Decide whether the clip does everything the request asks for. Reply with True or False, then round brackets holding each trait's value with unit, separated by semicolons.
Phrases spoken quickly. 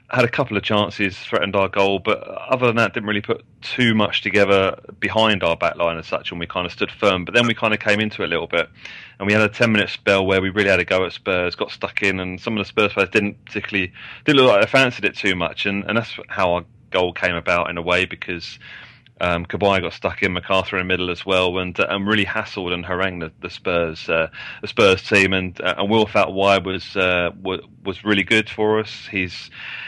True (250 wpm)